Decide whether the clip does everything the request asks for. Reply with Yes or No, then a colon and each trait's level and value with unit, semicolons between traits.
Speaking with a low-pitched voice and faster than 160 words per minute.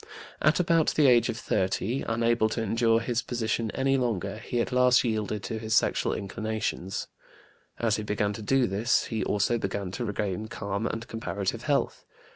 Yes: low, 110 Hz; average, 175 wpm